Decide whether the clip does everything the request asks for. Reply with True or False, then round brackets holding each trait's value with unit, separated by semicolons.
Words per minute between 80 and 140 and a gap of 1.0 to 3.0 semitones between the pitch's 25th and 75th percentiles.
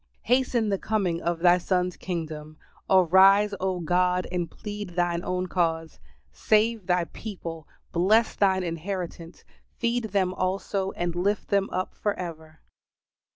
True (135 wpm; 2.7 semitones)